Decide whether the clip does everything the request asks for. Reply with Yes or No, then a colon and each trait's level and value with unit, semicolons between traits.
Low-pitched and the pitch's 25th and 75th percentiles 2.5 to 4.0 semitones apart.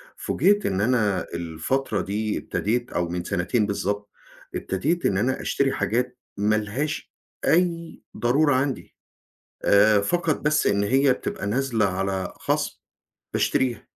No: low, 110 Hz; average, 5.1 semitones